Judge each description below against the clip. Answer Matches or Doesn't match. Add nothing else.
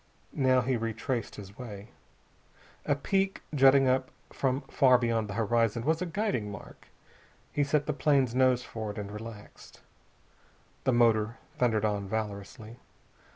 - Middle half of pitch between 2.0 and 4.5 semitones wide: Matches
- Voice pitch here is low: Matches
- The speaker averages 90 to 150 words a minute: Matches